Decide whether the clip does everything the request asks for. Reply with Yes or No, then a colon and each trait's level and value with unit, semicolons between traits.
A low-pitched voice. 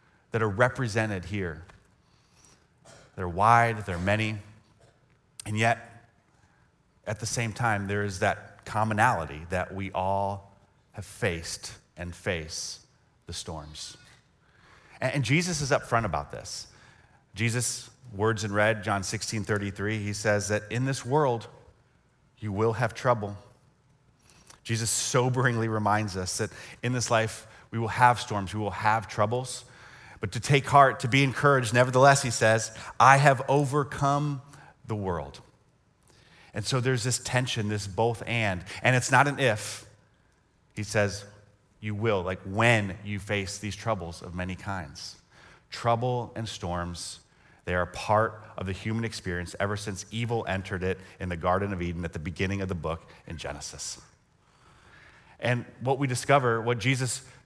Yes: low, 110 Hz